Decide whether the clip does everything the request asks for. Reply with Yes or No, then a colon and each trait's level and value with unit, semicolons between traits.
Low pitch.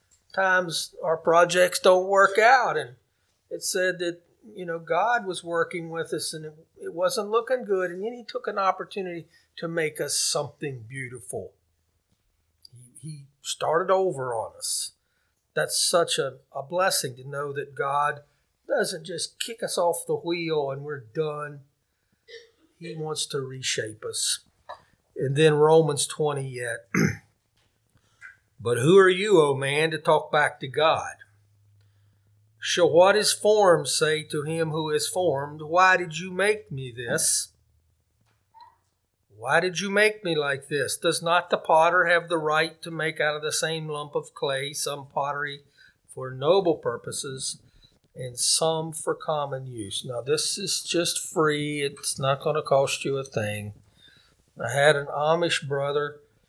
No: medium, 155 Hz